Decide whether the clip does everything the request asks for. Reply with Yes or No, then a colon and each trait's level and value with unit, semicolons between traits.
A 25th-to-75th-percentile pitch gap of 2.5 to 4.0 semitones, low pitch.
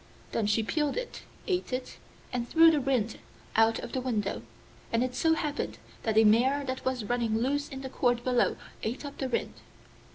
No: average, 3.7 semitones; very high, 255 Hz